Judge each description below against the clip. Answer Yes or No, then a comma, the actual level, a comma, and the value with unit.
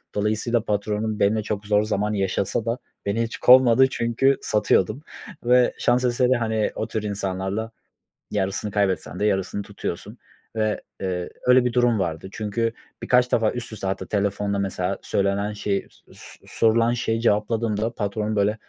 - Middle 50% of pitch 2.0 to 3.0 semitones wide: Yes, narrow, 2.5 semitones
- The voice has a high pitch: No, low, 105 Hz